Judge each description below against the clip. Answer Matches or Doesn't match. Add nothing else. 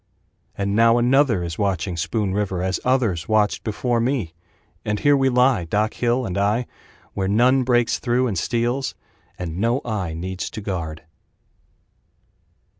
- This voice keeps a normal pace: Matches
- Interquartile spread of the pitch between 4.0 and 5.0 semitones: Matches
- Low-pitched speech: Matches